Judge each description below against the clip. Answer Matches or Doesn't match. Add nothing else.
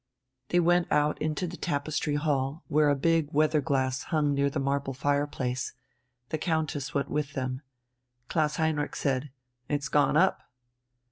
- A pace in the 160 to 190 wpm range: Doesn't match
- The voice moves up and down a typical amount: Doesn't match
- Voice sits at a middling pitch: Matches